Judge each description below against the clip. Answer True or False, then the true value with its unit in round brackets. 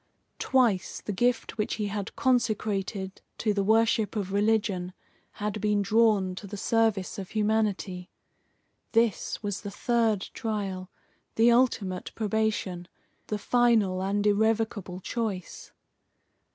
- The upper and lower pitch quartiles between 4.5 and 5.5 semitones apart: False (2.5 semitones)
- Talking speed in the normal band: False (120 wpm)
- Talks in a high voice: True (210 Hz)